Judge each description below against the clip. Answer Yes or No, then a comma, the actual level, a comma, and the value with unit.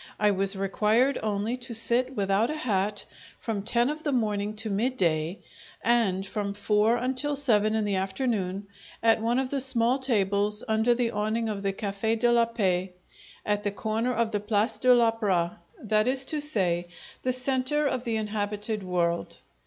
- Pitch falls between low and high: No, high, 220 Hz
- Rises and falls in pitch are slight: No, average, 3.3 semitones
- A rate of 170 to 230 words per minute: Yes, average, 175 wpm